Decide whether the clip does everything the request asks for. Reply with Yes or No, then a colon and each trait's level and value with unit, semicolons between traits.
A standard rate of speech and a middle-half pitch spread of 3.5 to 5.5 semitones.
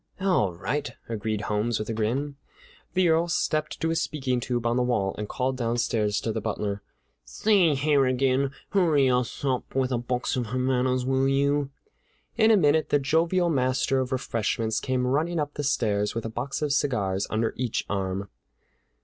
Yes: average, 175 wpm; average, 4.3 semitones